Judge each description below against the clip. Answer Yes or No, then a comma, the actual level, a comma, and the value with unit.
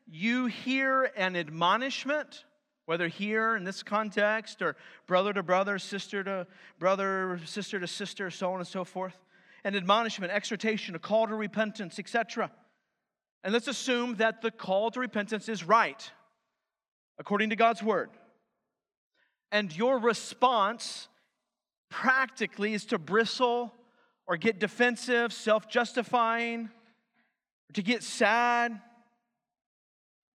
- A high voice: Yes, high, 220 Hz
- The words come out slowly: Yes, slow, 120 wpm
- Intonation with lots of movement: No, average, 3.1 semitones